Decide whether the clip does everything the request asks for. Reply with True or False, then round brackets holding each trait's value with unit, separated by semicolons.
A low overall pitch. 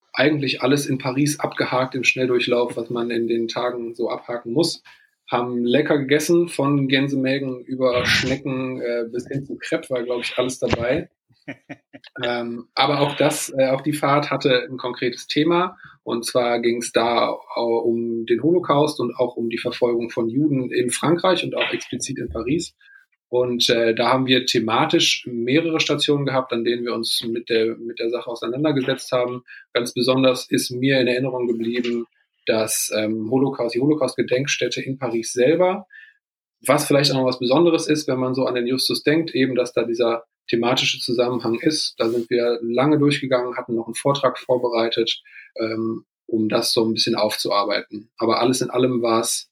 True (125 Hz)